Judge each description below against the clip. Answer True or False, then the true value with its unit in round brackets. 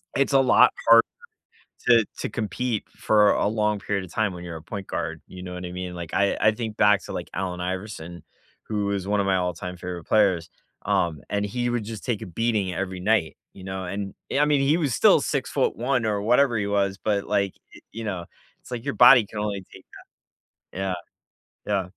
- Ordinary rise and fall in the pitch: True (3.4 semitones)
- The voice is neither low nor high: False (100 Hz)